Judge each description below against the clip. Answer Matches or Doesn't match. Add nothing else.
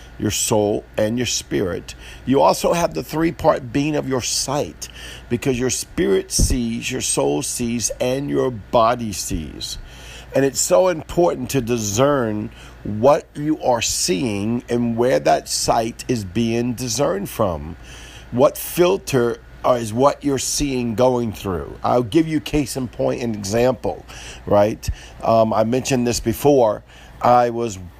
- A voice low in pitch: Matches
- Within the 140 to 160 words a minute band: Matches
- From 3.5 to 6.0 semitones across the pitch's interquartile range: Matches